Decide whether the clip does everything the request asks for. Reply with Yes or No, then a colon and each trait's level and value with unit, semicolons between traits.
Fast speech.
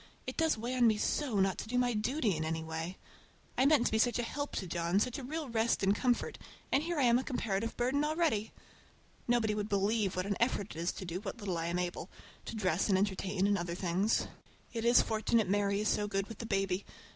Yes: fast, 240 wpm